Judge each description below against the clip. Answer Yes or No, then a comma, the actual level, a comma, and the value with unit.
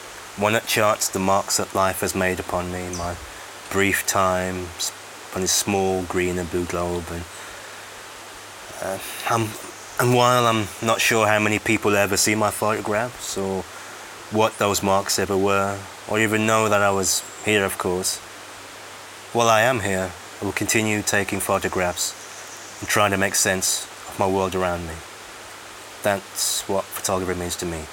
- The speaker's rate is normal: Yes, average, 165 wpm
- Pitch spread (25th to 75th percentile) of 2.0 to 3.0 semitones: Yes, narrow, 2.6 semitones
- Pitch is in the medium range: No, very low, 95 Hz